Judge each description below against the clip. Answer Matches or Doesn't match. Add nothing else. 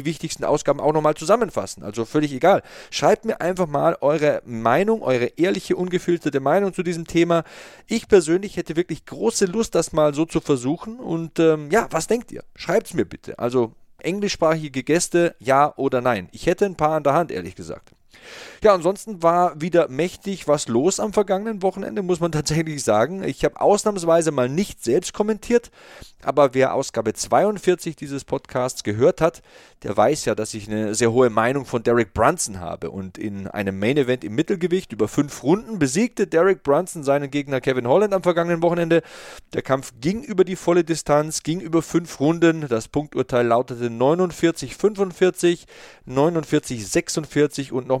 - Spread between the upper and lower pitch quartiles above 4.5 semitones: Matches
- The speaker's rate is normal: Matches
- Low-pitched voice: Doesn't match